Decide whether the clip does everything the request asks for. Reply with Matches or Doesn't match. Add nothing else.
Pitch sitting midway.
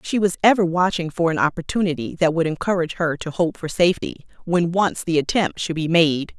Matches